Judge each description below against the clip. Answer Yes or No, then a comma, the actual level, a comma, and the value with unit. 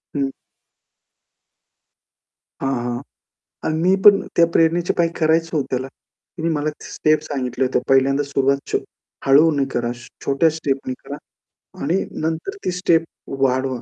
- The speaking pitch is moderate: Yes, medium, 145 Hz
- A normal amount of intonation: Yes, average, 3.5 semitones